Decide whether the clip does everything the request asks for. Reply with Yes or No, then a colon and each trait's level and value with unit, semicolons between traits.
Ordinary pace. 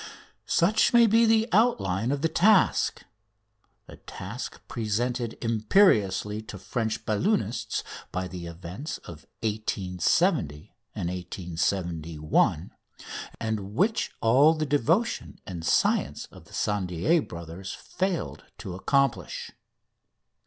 No: slow, 105 wpm